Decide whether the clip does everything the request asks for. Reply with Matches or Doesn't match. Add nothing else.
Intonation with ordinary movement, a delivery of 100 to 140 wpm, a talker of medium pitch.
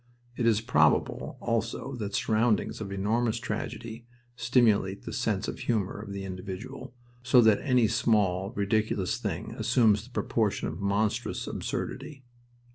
Doesn't match